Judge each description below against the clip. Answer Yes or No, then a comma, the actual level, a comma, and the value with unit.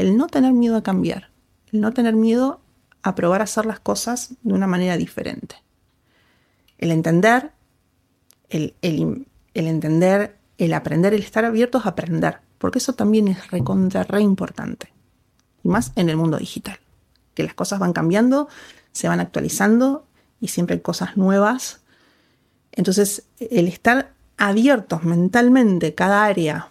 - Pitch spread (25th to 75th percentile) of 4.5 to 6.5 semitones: Yes, average, 5.0 semitones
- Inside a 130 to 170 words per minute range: Yes, average, 150 wpm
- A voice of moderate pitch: No, high, 205 Hz